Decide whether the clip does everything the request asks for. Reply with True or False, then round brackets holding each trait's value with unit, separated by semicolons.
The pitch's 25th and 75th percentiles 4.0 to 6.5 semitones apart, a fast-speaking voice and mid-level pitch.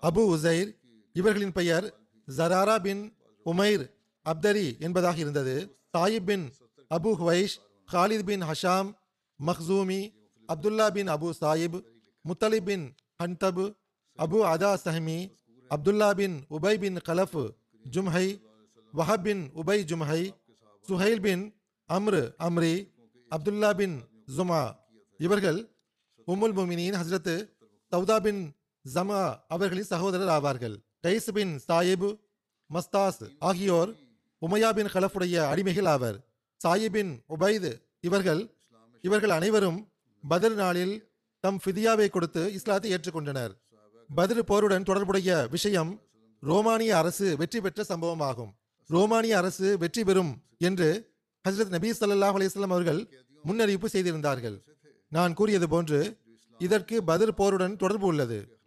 False (4.4 semitones; 105 wpm; 180 Hz)